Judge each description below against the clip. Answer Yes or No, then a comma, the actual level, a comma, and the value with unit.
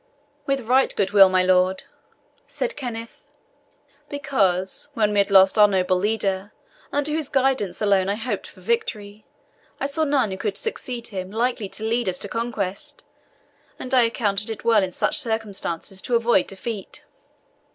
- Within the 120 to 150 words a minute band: No, average, 160 wpm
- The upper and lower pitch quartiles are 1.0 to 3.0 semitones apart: No, average, 4.2 semitones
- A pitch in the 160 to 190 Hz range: No, high, 215 Hz